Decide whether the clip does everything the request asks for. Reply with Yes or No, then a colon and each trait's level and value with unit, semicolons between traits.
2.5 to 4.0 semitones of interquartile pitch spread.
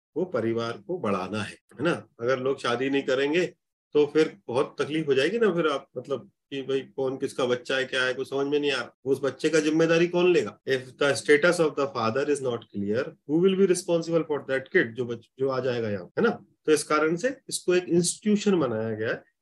No: average, 4.7 semitones